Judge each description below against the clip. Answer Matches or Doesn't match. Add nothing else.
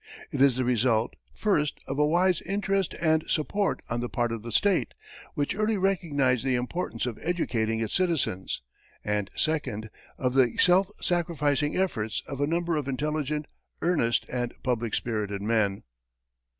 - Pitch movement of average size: Doesn't match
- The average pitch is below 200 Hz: Matches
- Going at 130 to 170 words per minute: Matches